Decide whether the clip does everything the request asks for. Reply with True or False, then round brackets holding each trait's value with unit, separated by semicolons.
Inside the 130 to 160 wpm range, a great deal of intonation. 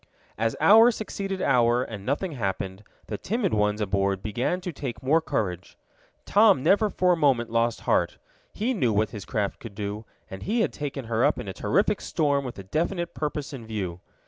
False (195 wpm; 8.9 semitones)